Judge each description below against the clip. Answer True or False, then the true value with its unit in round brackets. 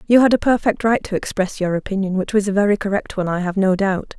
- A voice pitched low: False (200 Hz)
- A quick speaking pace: True (275 wpm)